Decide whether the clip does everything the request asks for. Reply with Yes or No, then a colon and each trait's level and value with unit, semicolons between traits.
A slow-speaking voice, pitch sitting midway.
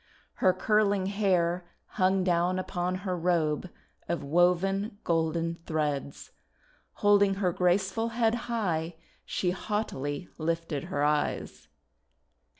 Yes: slow, 105 wpm; medium, 180 Hz